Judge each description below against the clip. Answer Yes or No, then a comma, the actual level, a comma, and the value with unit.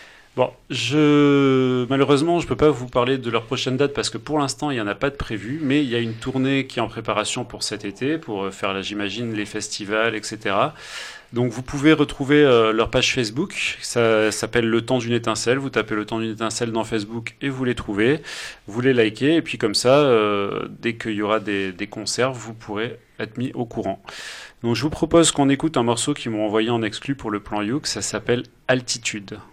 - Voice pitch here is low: Yes, low, 120 Hz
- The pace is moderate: No, fast, 225 wpm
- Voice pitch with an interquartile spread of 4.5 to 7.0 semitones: No, average, 3.8 semitones